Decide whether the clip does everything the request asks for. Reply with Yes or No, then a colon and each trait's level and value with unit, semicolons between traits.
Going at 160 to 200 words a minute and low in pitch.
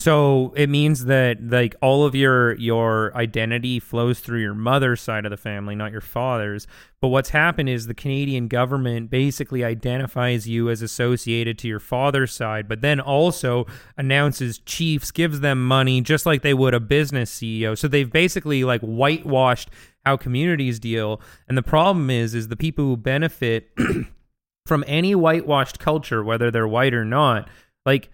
Yes: average, 170 wpm; low, 125 Hz